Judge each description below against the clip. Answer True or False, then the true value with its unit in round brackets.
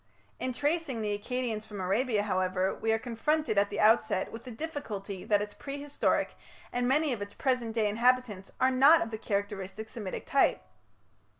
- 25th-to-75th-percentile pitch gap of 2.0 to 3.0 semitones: False (4.0 semitones)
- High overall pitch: True (225 Hz)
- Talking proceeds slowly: False (175 wpm)